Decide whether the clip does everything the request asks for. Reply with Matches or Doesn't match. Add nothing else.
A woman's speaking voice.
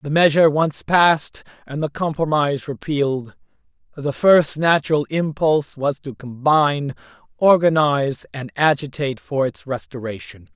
Doesn't match